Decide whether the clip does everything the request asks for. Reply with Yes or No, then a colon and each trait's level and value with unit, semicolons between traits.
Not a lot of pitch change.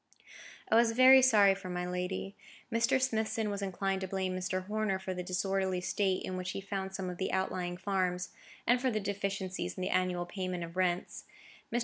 Yes: narrow, 1.9 semitones